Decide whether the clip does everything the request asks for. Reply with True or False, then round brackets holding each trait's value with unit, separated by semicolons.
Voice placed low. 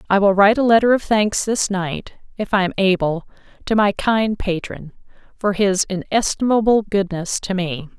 False (200 Hz)